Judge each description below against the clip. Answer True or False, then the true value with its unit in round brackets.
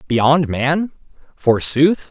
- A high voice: False (145 Hz)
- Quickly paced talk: False (85 wpm)